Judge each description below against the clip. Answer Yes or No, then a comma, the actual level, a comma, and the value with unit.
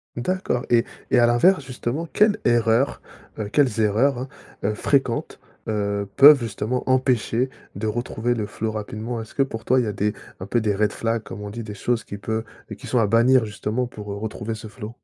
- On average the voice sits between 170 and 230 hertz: No, low, 115 Hz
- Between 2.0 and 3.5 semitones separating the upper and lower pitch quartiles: Yes, average, 2.9 semitones